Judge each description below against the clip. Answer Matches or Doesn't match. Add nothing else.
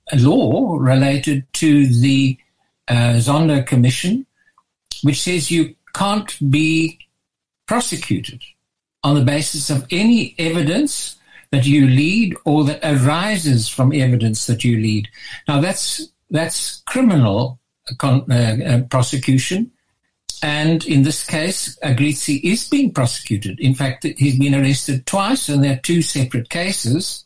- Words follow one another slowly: Matches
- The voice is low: Doesn't match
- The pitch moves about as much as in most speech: Matches